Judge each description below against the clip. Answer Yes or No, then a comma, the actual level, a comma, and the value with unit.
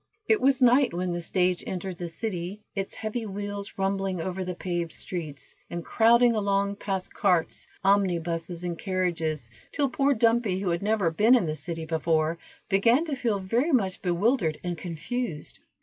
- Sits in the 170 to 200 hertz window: Yes, high, 190 Hz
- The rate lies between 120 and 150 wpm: No, average, 165 wpm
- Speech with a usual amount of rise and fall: Yes, average, 4.3 semitones